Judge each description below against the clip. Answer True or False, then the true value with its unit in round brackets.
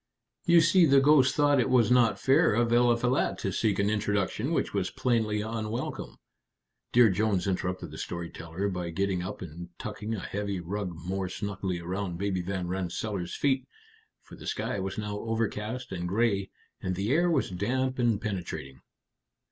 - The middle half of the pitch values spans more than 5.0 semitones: False (4.3 semitones)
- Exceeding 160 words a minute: True (170 wpm)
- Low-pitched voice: True (105 Hz)